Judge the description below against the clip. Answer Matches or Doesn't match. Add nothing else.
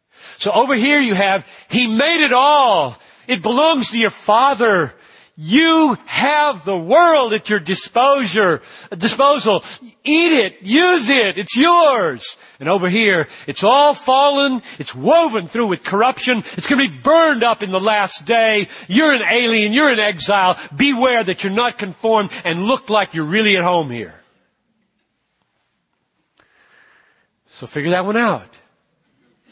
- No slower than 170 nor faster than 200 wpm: Doesn't match